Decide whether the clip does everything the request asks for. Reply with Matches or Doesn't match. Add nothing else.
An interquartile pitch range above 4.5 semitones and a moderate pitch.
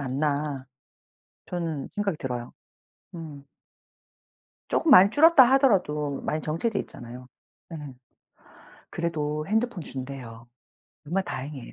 Matches